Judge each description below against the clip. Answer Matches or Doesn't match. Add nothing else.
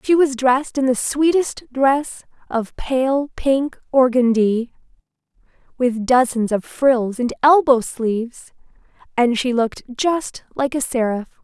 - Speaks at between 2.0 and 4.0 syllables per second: Matches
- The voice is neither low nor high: Doesn't match